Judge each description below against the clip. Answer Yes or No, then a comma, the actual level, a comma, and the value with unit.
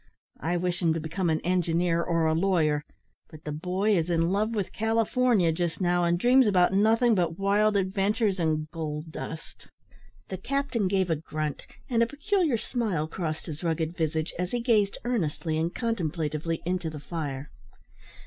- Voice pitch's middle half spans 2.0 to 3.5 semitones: No, average, 4.6 semitones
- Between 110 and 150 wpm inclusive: No, average, 170 wpm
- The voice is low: No, medium, 175 Hz